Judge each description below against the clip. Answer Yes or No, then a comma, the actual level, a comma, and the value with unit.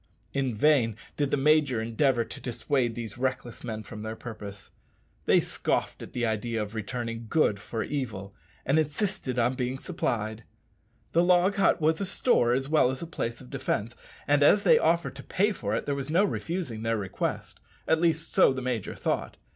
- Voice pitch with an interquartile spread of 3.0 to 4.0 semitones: No, average, 5.3 semitones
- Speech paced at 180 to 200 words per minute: Yes, average, 190 wpm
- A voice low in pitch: Yes, low, 125 Hz